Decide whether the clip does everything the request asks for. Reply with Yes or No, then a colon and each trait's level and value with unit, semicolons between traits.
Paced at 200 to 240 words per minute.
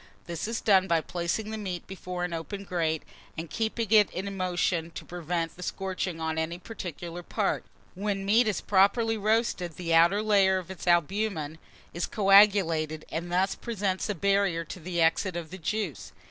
No: average, 175 wpm